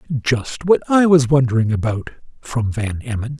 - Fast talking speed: No, average, 160 wpm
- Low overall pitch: Yes, low, 130 Hz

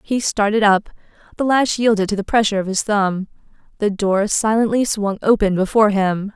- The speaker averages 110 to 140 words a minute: No, average, 180 wpm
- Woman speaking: Yes, female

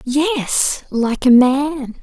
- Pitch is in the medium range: No, very high, 265 Hz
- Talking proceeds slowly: Yes, slow, 120 wpm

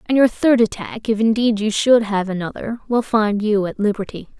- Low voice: No, high, 220 Hz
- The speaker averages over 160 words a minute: Yes, fast, 205 wpm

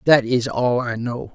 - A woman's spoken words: No, male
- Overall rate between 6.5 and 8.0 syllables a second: No, 4.1 syllables/s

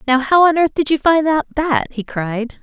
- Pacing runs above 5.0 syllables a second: No, 4.9 syllables/s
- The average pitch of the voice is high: Yes, very high, 285 Hz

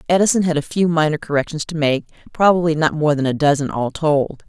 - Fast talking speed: Yes, fast, 215 wpm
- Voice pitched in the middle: Yes, medium, 155 Hz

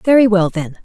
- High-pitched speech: Yes, high, 200 Hz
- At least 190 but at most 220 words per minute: Yes, fast, 215 wpm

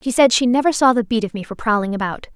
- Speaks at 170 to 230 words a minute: No, fast, 305 wpm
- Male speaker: No, female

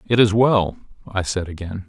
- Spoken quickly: No, average, 190 wpm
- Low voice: Yes, low, 100 Hz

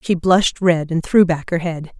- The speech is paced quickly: Yes, fast, 240 wpm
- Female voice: Yes, female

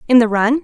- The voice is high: Yes, high, 240 Hz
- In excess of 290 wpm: No, fast, 280 wpm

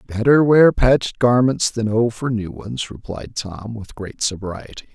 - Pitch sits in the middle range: No, low, 110 Hz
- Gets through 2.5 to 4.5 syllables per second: Yes, 4.4 syllables/s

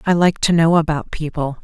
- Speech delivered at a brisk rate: Yes, fast, 220 wpm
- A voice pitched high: No, medium, 160 Hz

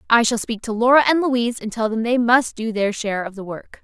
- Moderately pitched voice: No, high, 230 Hz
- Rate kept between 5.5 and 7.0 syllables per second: Yes, 5.9 syllables/s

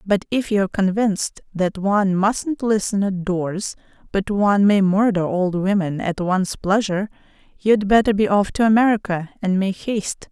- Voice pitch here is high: Yes, high, 200 Hz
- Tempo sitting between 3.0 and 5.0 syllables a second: Yes, 4.9 syllables/s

